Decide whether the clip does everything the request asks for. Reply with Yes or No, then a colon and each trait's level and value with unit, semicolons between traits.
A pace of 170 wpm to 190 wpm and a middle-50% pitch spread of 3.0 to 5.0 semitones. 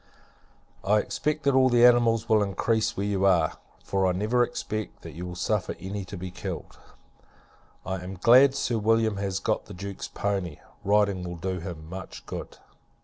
Yes: average, 175 wpm; average, 3.5 semitones